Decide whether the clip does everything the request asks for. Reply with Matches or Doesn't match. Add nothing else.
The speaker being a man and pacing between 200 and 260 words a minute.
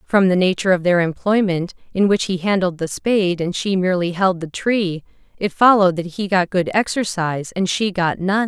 Doesn't match